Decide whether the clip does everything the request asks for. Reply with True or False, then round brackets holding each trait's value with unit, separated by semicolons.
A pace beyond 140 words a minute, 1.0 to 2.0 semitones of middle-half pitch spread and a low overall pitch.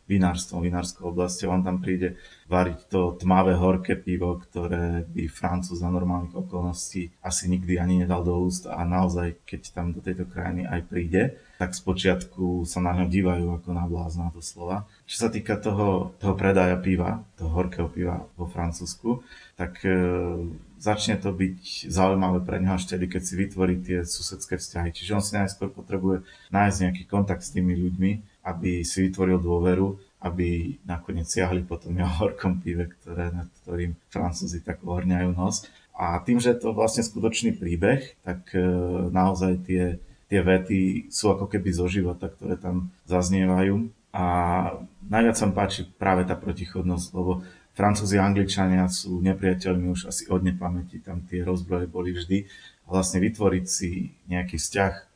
True (165 wpm; 1.3 semitones; 90 Hz)